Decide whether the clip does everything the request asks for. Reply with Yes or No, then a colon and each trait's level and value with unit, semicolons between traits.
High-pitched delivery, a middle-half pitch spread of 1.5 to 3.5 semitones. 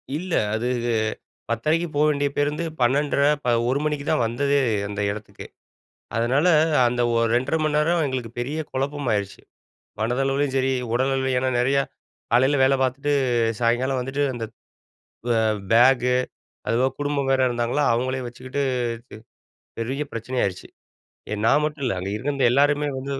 No: low, 130 Hz; average, 2.9 semitones